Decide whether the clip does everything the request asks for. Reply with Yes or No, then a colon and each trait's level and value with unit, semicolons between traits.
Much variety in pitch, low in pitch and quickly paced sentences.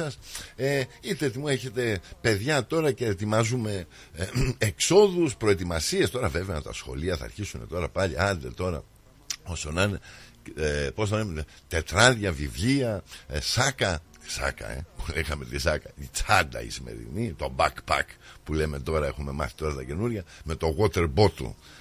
No: wide, 6.9 semitones; very low, 95 Hz; average, 150 wpm